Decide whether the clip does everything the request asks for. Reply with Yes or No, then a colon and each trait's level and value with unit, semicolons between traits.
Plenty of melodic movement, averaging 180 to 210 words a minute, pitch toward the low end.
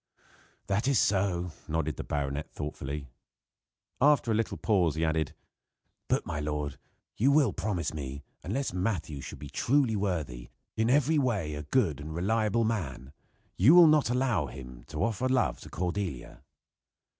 No: wide, 7.7 semitones; average, 155 wpm; very low, 90 Hz